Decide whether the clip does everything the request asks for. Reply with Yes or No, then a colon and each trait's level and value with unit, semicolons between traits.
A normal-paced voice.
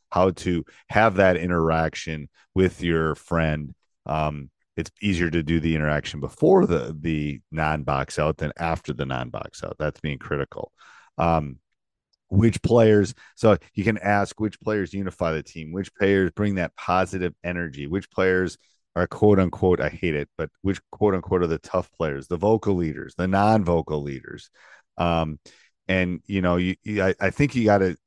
Yes: average, 175 wpm